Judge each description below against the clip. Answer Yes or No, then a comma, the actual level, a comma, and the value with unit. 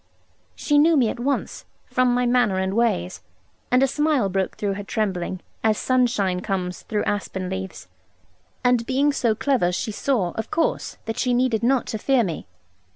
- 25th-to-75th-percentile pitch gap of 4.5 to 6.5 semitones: Yes, average, 4.9 semitones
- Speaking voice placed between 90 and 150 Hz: No, high, 225 Hz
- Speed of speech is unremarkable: Yes, average, 175 wpm